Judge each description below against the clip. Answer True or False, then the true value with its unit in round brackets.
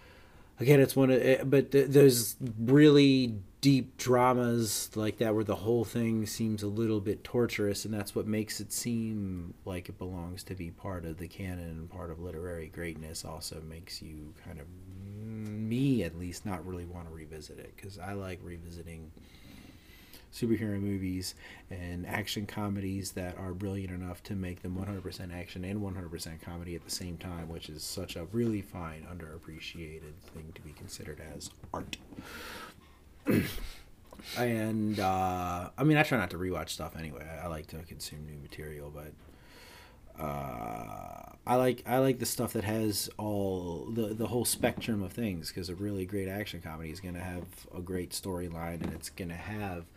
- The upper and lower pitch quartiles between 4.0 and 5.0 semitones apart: True (4.4 semitones)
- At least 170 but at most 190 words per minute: True (180 wpm)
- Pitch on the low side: True (95 Hz)